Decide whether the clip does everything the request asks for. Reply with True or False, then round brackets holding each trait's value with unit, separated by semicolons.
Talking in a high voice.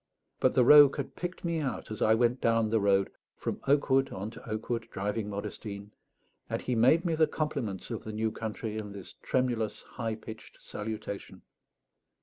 False (110 Hz)